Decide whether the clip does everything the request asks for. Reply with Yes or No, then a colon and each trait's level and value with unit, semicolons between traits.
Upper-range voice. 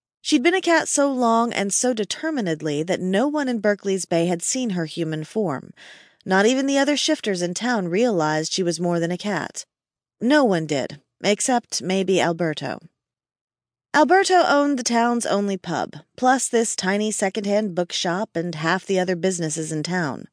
Yes: high, 200 Hz